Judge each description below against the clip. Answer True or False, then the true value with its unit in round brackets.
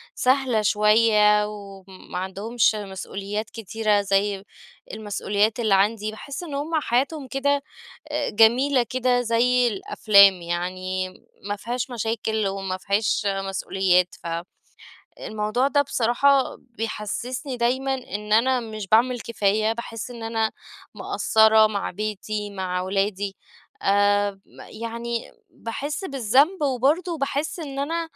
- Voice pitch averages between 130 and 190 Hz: False (220 Hz)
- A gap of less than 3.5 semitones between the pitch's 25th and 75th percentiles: False (3.8 semitones)